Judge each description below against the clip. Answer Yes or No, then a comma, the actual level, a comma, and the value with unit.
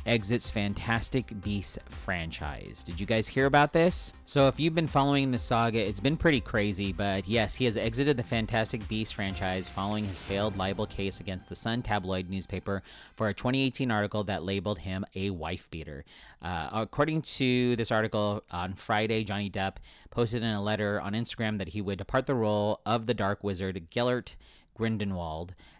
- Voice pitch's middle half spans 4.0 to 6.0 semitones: No, average, 3.5 semitones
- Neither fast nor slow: Yes, average, 180 wpm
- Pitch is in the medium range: No, low, 105 Hz